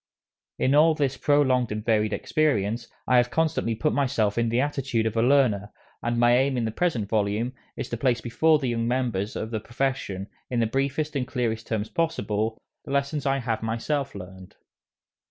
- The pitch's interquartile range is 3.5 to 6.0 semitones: Yes, average, 3.8 semitones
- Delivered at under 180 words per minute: No, average, 190 wpm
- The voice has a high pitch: No, low, 120 Hz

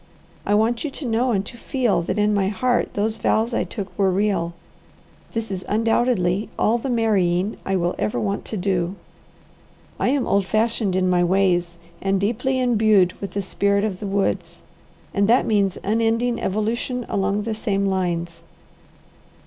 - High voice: Yes, high, 200 Hz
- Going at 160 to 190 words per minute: Yes, average, 170 wpm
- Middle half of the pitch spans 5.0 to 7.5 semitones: No, average, 3.3 semitones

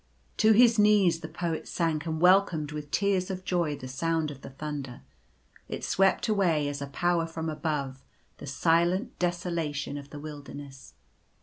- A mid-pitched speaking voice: Yes, medium, 160 Hz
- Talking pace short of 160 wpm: No, average, 165 wpm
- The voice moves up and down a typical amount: Yes, average, 3.7 semitones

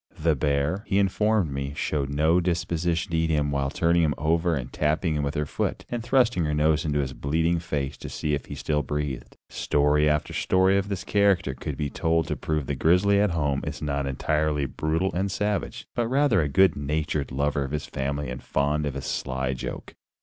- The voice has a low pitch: Yes, very low, 75 Hz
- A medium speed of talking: No, fast, 215 wpm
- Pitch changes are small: No, average, 3.4 semitones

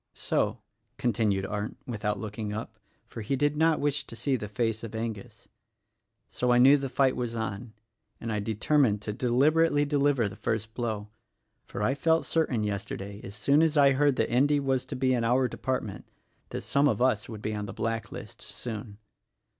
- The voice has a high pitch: No, low, 120 Hz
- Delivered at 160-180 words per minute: No, average, 200 wpm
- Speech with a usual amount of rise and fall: Yes, average, 4.4 semitones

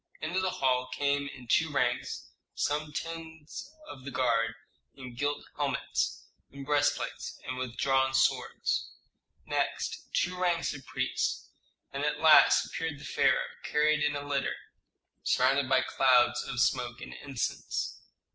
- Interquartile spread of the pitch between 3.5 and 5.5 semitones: No, narrow, 2.6 semitones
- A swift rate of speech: No, average, 140 wpm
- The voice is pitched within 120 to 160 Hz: Yes, medium, 140 Hz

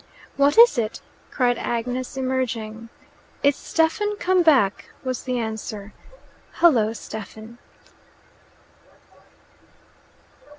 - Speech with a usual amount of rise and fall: Yes, average, 4.3 semitones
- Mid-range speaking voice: No, very high, 250 Hz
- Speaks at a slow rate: Yes, slow, 85 wpm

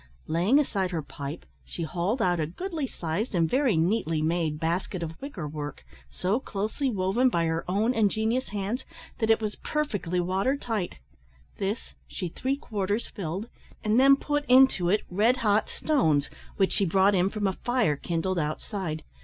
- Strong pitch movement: Yes, wide, 5.7 semitones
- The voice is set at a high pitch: Yes, high, 195 Hz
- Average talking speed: Yes, average, 170 wpm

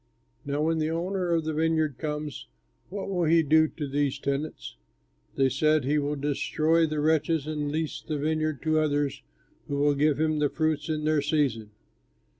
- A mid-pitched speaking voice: Yes, medium, 155 Hz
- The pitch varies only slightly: Yes, narrow, 1.5 semitones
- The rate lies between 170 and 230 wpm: Yes, average, 180 wpm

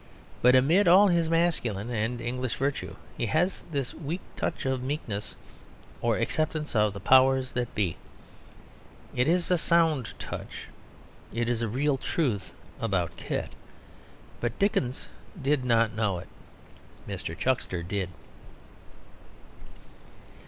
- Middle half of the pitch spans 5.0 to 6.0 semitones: Yes, wide, 5.5 semitones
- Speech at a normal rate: No, slow, 125 wpm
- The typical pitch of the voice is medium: No, low, 130 Hz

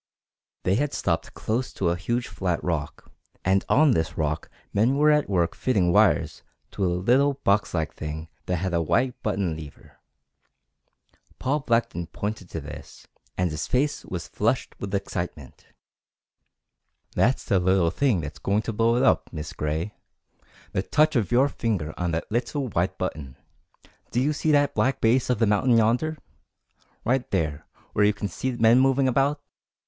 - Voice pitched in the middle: No, low, 105 Hz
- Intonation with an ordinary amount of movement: No, wide, 6.6 semitones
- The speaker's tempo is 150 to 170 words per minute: Yes, average, 165 wpm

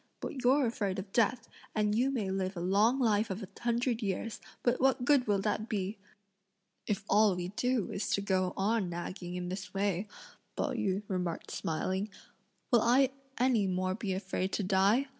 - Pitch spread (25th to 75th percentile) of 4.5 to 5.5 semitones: No, average, 3.8 semitones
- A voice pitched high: Yes, high, 205 Hz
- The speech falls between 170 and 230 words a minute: Yes, average, 180 wpm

